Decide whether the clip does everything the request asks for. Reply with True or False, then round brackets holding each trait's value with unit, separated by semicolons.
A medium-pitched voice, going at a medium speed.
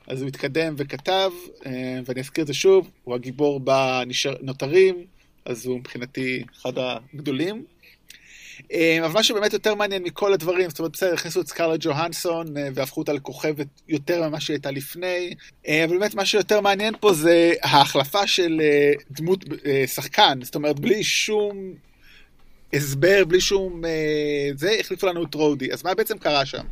False (160 Hz; 155 wpm)